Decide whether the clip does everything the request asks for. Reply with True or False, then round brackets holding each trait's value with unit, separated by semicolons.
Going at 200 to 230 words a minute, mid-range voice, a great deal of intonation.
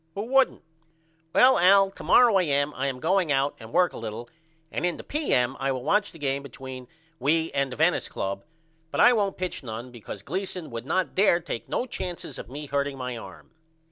True (205 wpm; 145 Hz; 6.5 semitones)